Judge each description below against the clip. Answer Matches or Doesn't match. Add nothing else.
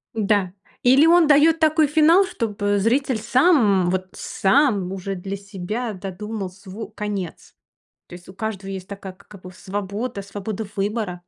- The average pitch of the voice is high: Matches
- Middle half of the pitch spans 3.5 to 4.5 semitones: Matches